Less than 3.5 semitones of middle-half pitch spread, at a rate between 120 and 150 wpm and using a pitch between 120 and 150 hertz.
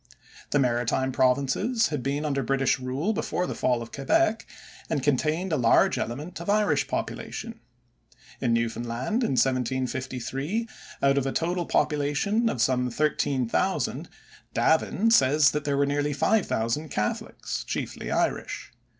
No: average, 4.2 semitones; average, 140 wpm; medium, 140 Hz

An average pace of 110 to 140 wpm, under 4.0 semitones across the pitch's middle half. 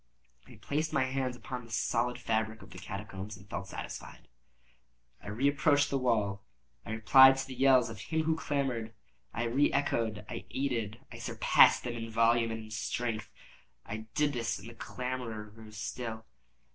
No: average, 165 wpm; average, 3.2 semitones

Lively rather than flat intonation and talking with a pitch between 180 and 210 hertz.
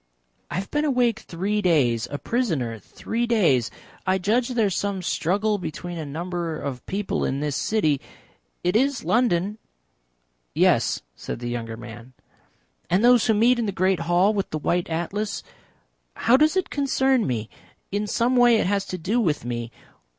Yes: wide, 6.8 semitones; high, 190 Hz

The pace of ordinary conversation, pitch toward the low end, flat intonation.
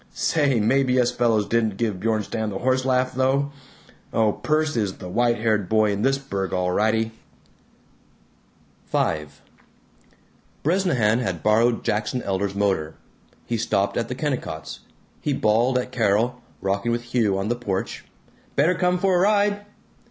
No: average, 150 wpm; low, 115 Hz; average, 4.1 semitones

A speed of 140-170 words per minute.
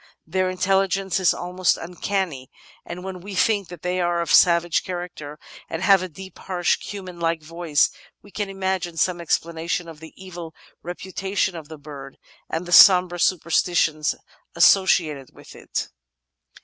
Yes: average, 160 wpm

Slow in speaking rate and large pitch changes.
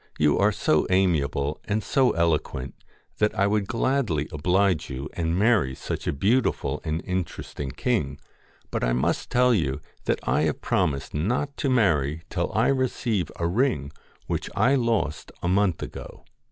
No: average, 160 wpm; wide, 7.1 semitones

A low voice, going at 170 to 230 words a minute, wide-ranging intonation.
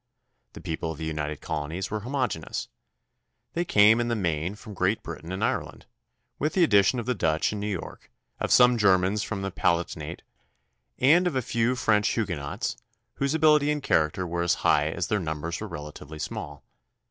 Yes: very low, 95 Hz; average, 180 wpm; wide, 6.7 semitones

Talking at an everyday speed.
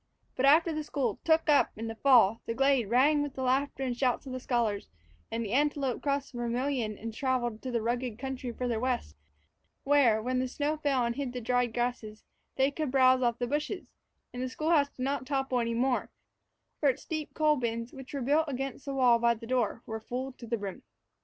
No: fast, 220 wpm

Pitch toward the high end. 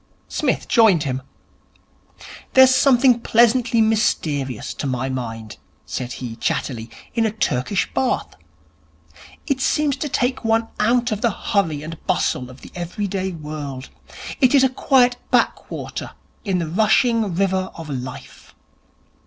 Yes: high, 195 Hz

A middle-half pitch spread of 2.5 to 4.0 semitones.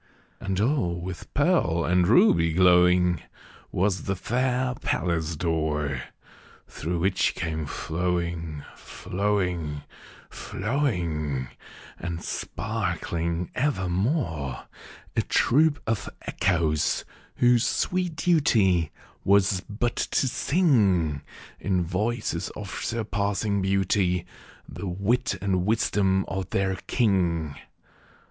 No: average, 4.4 semitones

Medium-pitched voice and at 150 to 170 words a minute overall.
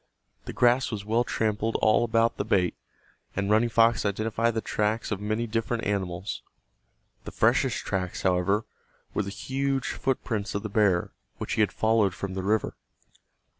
No: low, 110 Hz; average, 165 wpm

